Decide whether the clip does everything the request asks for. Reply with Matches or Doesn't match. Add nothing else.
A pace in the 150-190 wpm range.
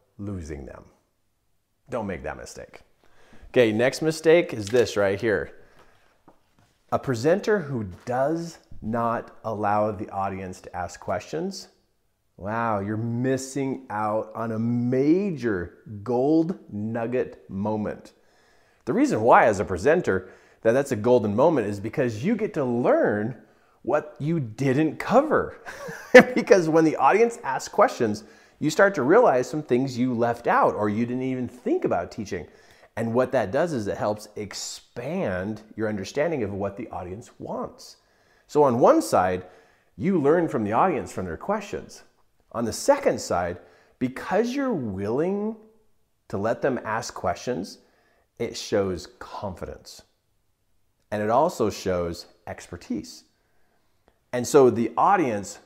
Doesn't match